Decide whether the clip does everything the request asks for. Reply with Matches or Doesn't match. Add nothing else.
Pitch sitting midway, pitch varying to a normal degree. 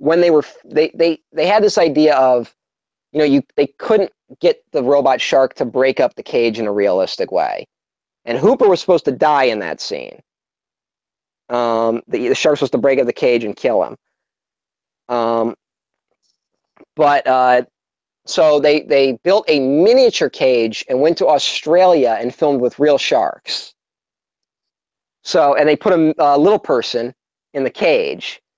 Doesn't match